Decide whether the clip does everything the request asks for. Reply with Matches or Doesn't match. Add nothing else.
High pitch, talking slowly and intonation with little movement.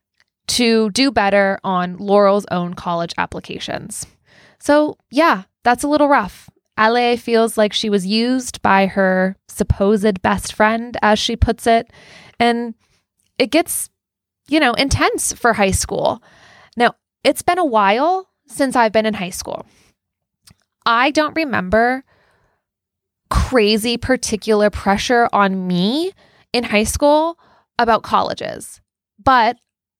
Doesn't match